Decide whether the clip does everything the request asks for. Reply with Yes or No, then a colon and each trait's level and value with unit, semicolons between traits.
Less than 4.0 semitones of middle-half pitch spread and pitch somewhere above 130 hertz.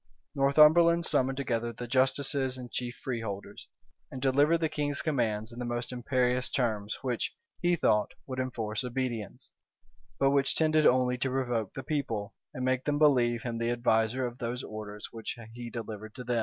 No: average, 2.7 semitones; low, 125 Hz